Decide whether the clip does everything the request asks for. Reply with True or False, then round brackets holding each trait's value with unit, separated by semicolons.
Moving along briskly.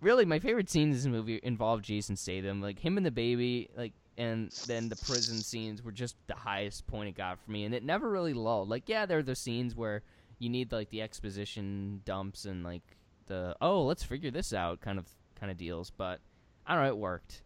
True (230 wpm)